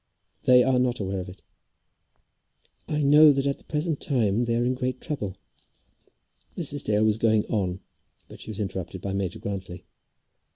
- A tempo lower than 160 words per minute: No, average, 170 wpm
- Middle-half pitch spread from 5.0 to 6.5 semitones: Yes, wide, 5.5 semitones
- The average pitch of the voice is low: Yes, low, 115 Hz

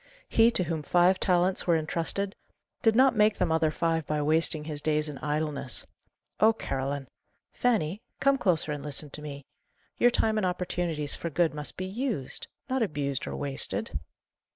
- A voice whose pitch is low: No, medium, 165 Hz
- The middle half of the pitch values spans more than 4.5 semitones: Yes, average, 4.9 semitones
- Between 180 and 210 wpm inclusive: No, average, 170 wpm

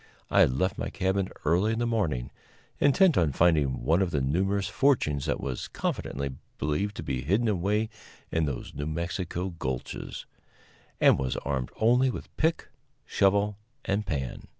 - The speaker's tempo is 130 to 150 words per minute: No, average, 160 wpm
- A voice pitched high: No, very low, 90 Hz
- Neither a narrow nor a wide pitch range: No, wide, 6.4 semitones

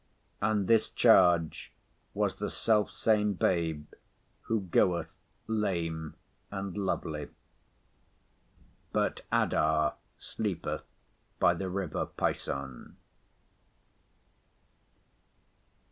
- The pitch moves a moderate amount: Yes, average, 4.5 semitones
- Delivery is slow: Yes, slow, 70 wpm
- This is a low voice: Yes, very low, 90 Hz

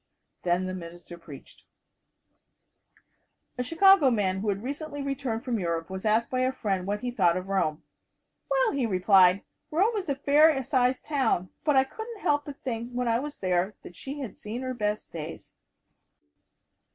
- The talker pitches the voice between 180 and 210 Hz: No, high, 235 Hz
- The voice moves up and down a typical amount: No, wide, 7.0 semitones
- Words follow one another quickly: No, average, 175 wpm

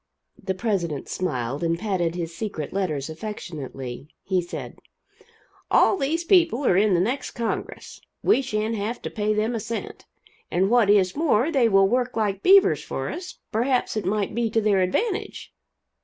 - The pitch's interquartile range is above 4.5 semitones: Yes, average, 4.9 semitones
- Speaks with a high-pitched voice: Yes, high, 210 Hz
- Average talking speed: Yes, average, 170 wpm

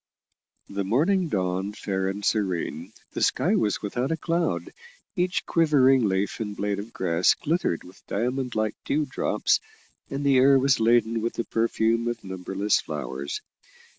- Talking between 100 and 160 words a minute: Yes, average, 155 wpm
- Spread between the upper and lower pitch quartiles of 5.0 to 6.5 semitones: Yes, wide, 5.4 semitones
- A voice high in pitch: No, low, 110 Hz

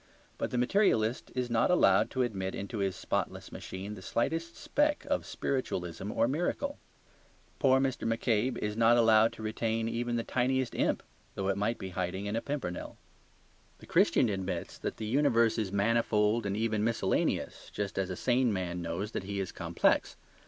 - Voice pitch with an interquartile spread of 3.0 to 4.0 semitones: Yes, average, 3.7 semitones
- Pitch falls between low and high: No, low, 115 Hz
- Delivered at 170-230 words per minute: Yes, average, 175 wpm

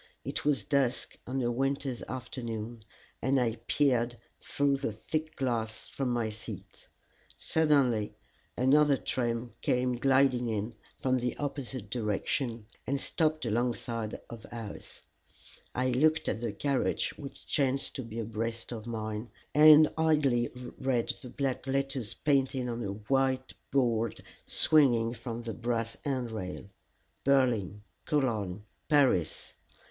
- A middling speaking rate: No, slow, 125 wpm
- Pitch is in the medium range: No, low, 125 Hz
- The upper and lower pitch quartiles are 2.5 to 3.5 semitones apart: Yes, average, 3.1 semitones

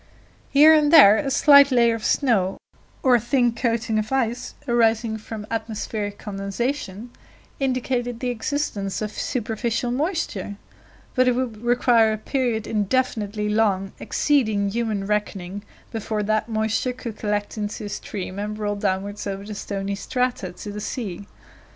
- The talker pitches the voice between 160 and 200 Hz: No, high, 220 Hz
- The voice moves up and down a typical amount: Yes, average, 3.2 semitones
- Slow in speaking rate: No, average, 145 wpm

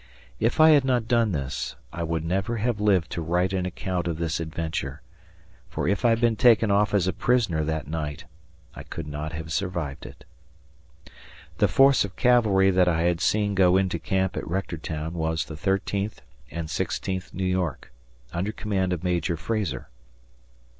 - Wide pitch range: No, average, 4.0 semitones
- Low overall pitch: Yes, very low, 90 Hz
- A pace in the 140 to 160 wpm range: No, average, 175 wpm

